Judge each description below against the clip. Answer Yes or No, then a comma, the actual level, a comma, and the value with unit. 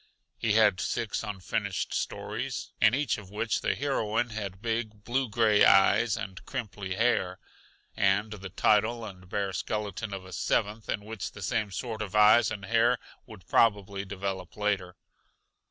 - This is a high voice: No, low, 105 Hz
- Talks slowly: No, average, 155 wpm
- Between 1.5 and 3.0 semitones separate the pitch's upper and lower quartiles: Yes, narrow, 2.5 semitones